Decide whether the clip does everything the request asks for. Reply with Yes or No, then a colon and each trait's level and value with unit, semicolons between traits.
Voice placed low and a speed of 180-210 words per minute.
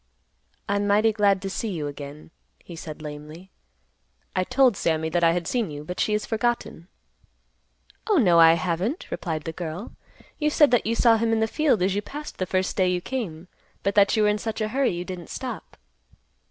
No: high, 190 Hz; fast, 205 wpm